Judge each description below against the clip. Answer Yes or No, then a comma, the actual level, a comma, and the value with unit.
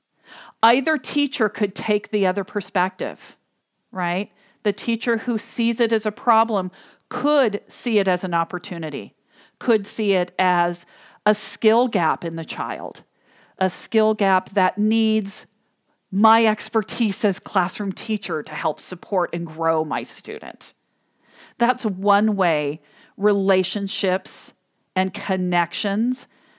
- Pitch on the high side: Yes, high, 205 Hz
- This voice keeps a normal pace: No, slow, 125 wpm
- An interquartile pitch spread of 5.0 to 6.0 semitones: No, average, 3.3 semitones